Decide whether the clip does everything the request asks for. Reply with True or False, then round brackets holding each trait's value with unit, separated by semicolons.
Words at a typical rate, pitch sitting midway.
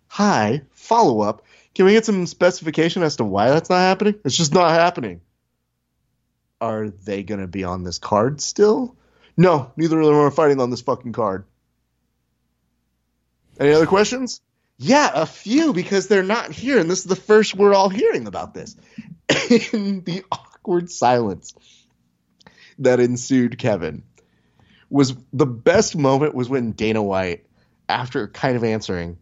True (155 wpm; 150 Hz)